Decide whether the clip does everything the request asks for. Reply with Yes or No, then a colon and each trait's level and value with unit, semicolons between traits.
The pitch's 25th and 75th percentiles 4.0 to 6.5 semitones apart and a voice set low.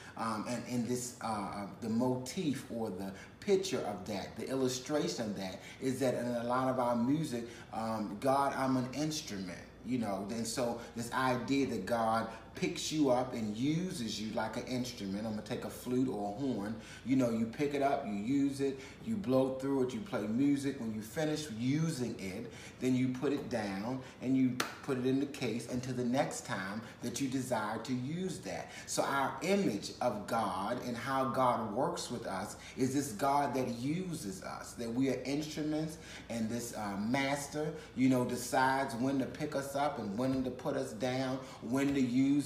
No: average, 2.8 semitones; low, 130 Hz